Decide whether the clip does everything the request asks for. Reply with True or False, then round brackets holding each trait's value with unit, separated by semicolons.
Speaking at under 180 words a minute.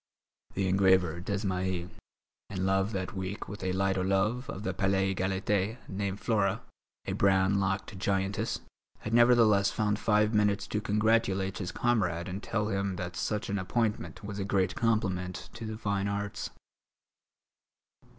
True (150 wpm)